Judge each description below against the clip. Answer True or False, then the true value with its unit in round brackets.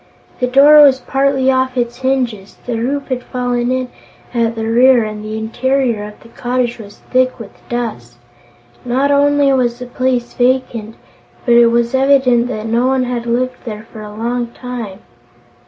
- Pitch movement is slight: True (2.1 semitones)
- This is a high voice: True (245 Hz)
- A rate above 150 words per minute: True (170 wpm)